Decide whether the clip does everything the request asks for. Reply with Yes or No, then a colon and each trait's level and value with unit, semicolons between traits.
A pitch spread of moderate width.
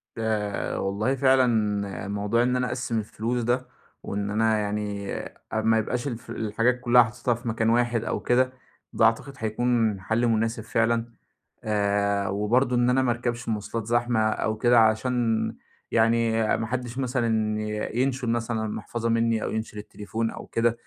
No: narrow, 2.0 semitones